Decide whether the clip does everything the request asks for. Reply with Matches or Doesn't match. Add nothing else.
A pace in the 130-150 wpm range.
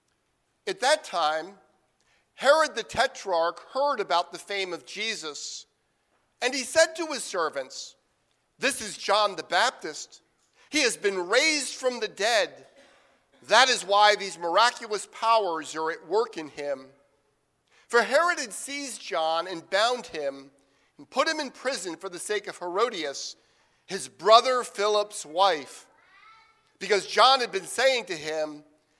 Matches